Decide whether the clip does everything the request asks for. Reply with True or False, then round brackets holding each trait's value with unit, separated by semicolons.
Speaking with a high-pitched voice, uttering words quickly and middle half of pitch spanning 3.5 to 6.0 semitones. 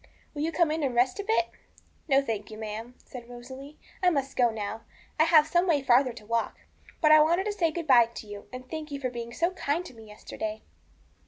True (270 Hz; 240 wpm; 5.3 semitones)